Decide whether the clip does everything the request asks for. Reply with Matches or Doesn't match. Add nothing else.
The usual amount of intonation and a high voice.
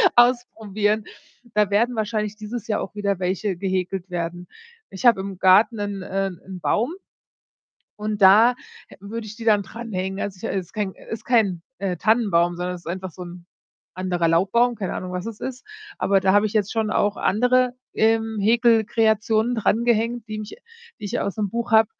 Matches